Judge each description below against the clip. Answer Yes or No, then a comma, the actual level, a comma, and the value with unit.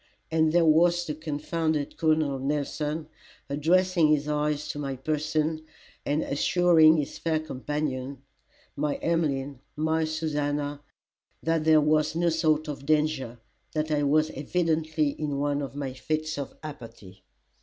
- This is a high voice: No, medium, 155 Hz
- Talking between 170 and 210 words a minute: No, slow, 135 wpm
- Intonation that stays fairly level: Yes, narrow, 1.6 semitones